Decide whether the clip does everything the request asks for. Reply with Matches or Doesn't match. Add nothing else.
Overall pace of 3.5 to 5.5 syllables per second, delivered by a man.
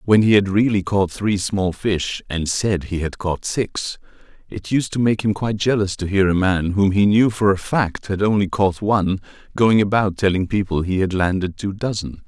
Matches